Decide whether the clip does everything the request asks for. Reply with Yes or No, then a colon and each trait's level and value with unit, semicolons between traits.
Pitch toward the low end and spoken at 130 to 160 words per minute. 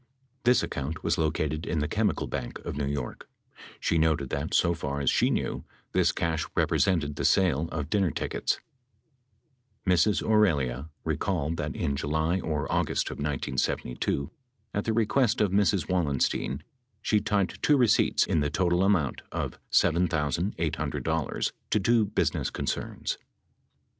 Yes: very low, 80 Hz; average, 145 wpm